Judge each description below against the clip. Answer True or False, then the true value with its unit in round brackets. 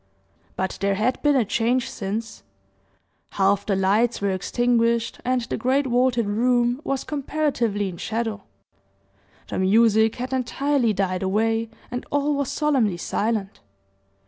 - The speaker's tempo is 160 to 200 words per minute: False (135 wpm)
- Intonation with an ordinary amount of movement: True (3.8 semitones)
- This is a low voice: False (230 Hz)